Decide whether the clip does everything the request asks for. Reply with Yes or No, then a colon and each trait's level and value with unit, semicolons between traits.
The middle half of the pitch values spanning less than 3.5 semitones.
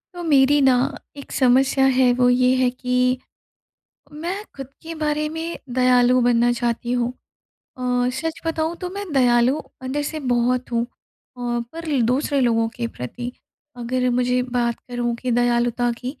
Yes: average, 2.8 semitones